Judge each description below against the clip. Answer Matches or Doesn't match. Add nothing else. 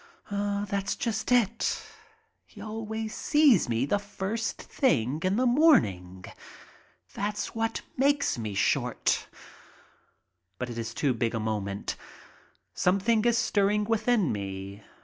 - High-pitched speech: Matches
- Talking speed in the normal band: Doesn't match